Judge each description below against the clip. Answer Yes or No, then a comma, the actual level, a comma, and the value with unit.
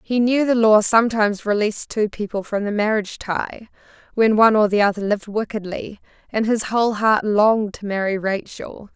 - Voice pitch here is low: No, high, 210 Hz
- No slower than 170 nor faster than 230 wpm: Yes, average, 180 wpm